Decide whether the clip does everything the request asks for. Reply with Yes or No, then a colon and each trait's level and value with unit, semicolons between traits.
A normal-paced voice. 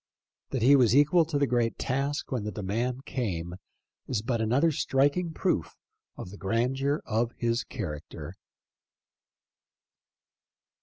No: slow, 125 wpm